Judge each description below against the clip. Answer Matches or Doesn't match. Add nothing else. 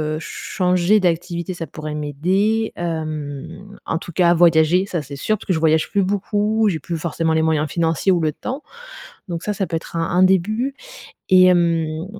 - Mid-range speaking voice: Matches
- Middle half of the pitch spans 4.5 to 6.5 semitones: Doesn't match